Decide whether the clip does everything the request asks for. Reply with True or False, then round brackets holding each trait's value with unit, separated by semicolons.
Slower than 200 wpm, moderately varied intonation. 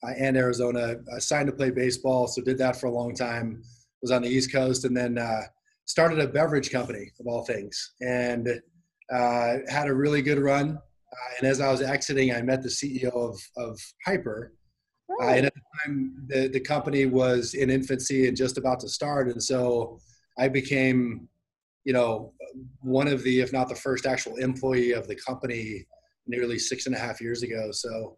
False (190 wpm; 1.8 semitones)